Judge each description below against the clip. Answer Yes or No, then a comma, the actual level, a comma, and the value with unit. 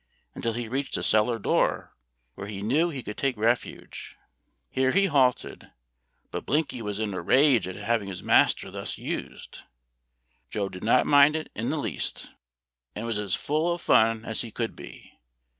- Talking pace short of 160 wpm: No, average, 175 wpm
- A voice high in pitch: No, low, 115 Hz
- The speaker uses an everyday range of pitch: Yes, average, 4.8 semitones